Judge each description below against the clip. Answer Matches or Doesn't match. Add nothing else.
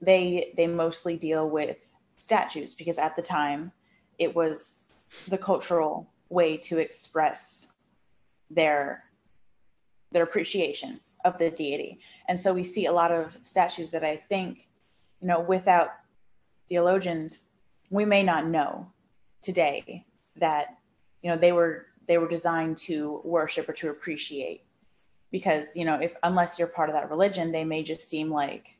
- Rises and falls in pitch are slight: Matches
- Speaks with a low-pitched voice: Doesn't match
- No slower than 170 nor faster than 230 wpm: Doesn't match